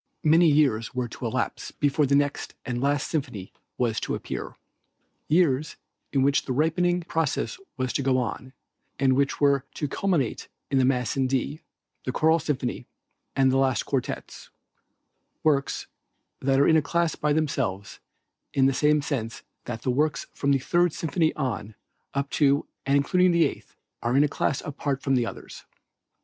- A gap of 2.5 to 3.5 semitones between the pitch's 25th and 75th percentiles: Yes, average, 2.9 semitones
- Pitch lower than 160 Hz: Yes, medium, 140 Hz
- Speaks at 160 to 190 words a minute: Yes, average, 170 wpm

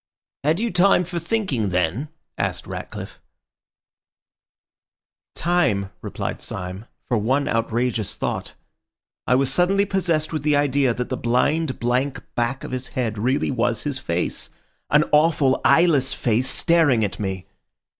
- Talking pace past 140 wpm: No, slow, 135 wpm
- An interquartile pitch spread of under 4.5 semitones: No, average, 5.2 semitones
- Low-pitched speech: Yes, low, 130 Hz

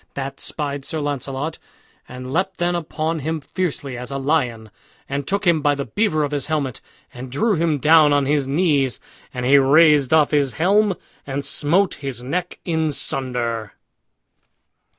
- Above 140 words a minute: Yes, average, 165 wpm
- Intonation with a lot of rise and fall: No, average, 3.2 semitones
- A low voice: No, medium, 145 Hz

